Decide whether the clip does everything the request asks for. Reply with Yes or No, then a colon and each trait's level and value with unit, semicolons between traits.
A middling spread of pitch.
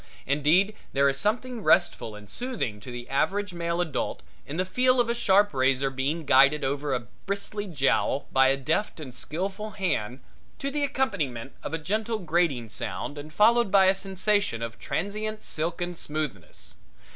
No: wide, 7.1 semitones